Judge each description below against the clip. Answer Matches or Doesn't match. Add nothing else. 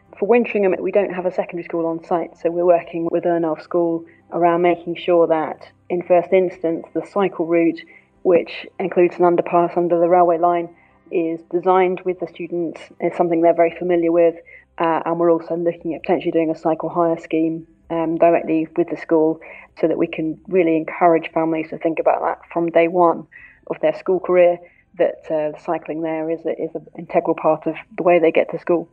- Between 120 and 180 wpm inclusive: Doesn't match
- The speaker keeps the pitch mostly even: Matches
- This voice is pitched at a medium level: Matches